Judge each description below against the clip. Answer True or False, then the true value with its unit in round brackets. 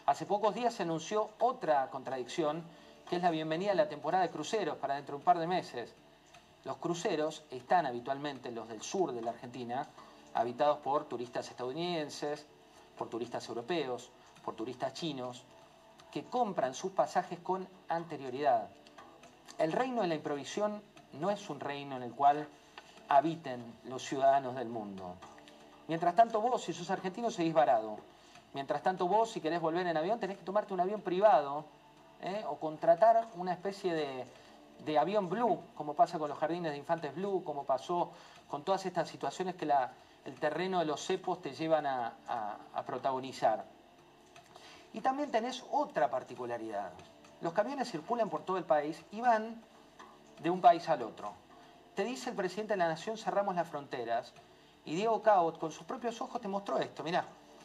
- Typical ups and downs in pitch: False (6.2 semitones)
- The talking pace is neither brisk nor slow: True (170 wpm)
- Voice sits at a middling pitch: True (165 Hz)